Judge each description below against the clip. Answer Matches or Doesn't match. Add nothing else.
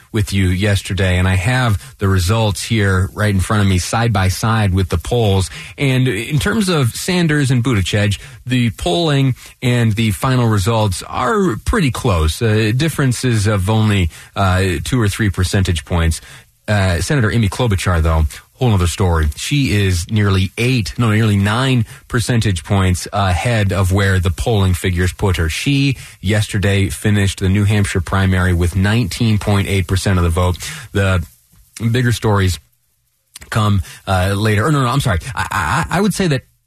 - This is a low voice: Matches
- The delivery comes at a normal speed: Matches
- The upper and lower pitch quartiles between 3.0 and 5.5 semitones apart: Matches